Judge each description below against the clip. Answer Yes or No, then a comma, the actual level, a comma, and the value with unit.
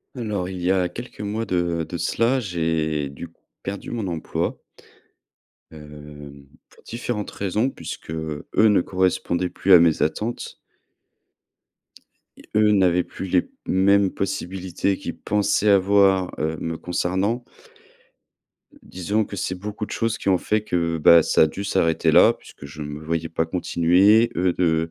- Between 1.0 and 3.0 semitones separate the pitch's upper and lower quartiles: No, average, 3.7 semitones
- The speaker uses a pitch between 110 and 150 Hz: No, very low, 90 Hz